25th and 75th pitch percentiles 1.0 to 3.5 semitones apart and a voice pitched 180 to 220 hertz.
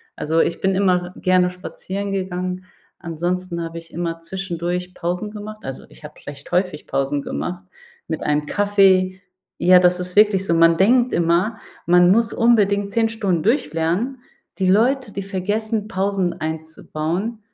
Yes: average, 3.2 semitones; medium, 185 Hz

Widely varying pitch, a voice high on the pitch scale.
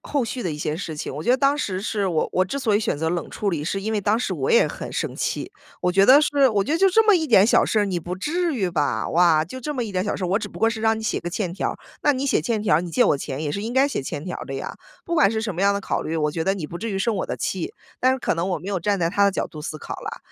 Yes: wide, 5.9 semitones; high, 200 Hz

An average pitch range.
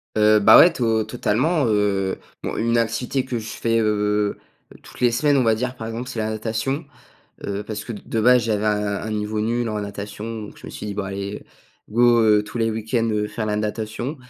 No: narrow, 2.0 semitones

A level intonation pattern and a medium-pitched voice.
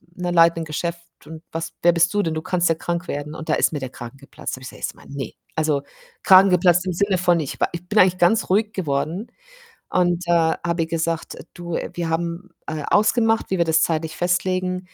Yes: narrow, 2.2 semitones; medium, 170 Hz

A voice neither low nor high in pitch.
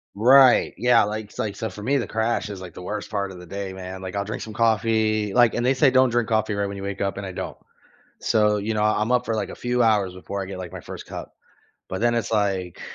No: low, 105 Hz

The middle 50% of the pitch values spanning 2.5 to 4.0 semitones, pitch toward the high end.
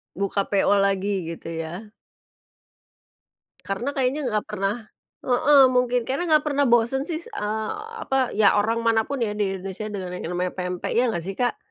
No: average, 4.5 semitones; high, 215 Hz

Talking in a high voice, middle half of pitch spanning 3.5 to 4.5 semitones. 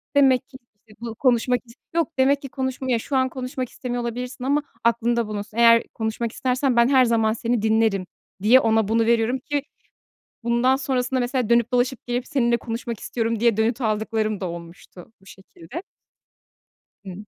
No: high, 235 Hz; narrow, 2.6 semitones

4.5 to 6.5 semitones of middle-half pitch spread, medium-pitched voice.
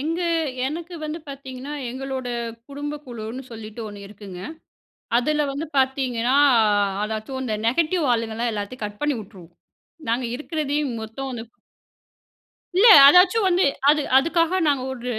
No: average, 4.8 semitones; very high, 265 Hz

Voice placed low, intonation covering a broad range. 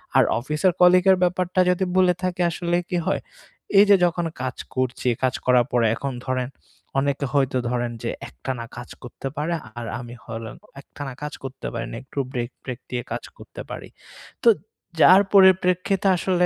No: medium, 145 Hz; wide, 6.2 semitones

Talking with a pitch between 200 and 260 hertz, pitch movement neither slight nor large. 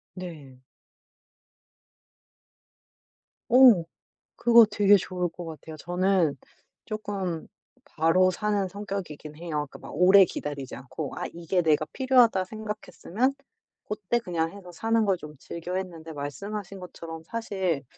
No: medium, 185 Hz; average, 4.2 semitones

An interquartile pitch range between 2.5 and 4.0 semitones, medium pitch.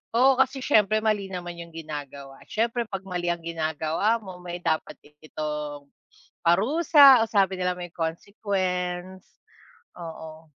No: average, 4.7 semitones; medium, 180 Hz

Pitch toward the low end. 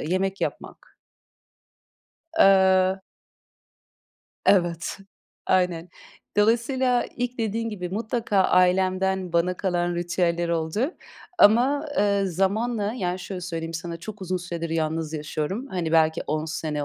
No: medium, 185 Hz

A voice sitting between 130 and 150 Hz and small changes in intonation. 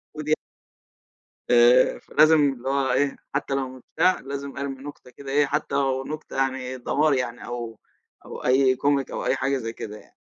Yes: low, 135 Hz; narrow, 1.8 semitones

